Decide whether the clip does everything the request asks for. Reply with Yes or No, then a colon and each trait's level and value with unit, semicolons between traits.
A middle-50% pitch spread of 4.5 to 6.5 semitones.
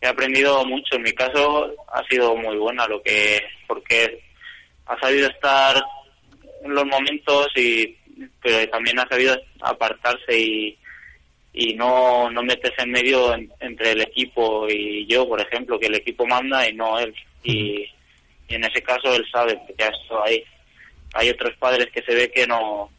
No: average, 2.9 semitones